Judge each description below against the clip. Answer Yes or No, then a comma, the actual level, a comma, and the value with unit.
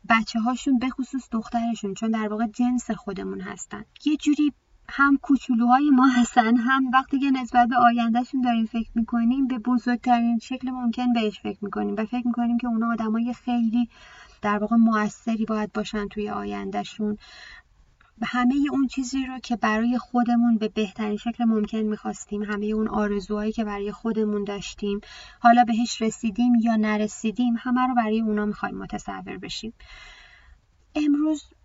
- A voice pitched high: Yes, high, 235 Hz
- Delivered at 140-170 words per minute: Yes, average, 150 wpm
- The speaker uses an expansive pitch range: No, narrow, 2.4 semitones